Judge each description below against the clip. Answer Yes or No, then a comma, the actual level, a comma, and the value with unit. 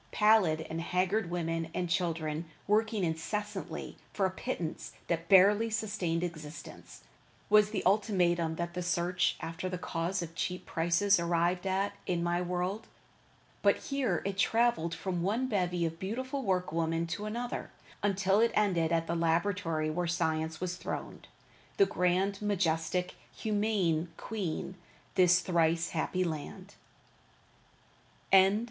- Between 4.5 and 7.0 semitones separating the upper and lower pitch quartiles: No, average, 3.4 semitones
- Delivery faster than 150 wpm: No, slow, 135 wpm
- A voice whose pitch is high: No, medium, 180 Hz